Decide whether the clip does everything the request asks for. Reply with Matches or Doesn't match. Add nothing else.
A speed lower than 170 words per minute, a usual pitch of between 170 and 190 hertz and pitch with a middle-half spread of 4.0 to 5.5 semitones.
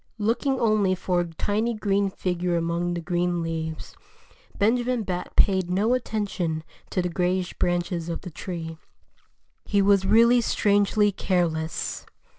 Doesn't match